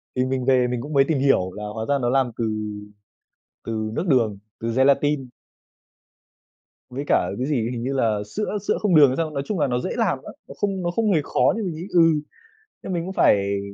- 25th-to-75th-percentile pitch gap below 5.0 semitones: No, wide, 5.5 semitones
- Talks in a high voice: No, low, 135 Hz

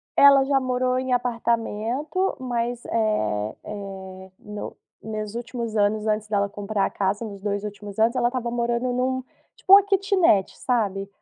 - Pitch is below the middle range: No, high, 230 Hz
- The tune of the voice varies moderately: Yes, average, 3.6 semitones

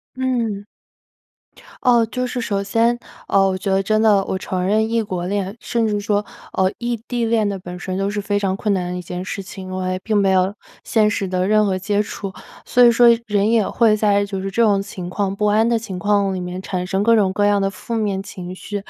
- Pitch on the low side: No, high, 205 Hz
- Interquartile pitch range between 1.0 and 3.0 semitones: Yes, narrow, 2.5 semitones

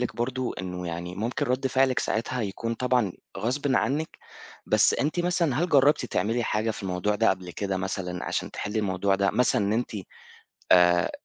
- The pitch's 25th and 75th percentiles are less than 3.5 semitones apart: No, average, 5.3 semitones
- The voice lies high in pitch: No, low, 110 Hz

